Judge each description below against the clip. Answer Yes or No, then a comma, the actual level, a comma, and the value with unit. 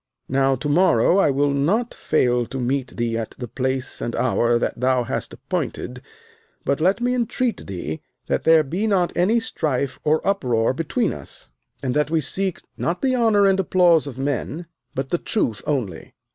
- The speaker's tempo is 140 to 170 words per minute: No, average, 180 wpm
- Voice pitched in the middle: Yes, medium, 145 Hz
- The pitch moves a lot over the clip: Yes, wide, 6.6 semitones